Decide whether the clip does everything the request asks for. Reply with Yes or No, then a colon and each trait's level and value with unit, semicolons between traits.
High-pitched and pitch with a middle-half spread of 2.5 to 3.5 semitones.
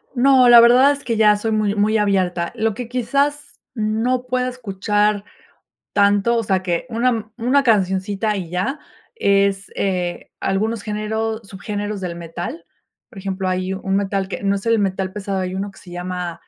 Yes: high, 205 Hz; average, 3.1 semitones